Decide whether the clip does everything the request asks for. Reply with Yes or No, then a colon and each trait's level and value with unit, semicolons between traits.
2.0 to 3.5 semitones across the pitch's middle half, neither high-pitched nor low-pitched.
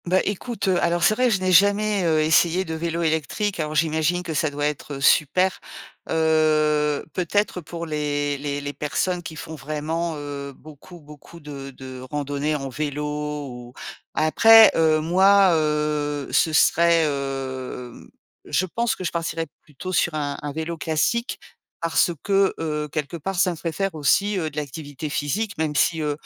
Yes: average, 3.0 semitones; medium, 155 Hz